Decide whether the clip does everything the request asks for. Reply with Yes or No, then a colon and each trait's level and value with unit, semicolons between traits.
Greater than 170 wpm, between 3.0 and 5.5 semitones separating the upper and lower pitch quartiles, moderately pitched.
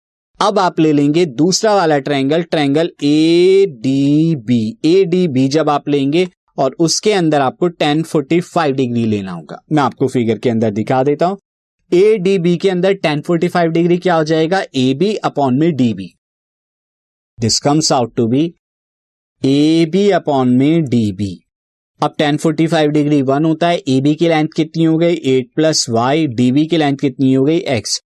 Yes: average, 185 wpm; average, 4.3 semitones; medium, 155 Hz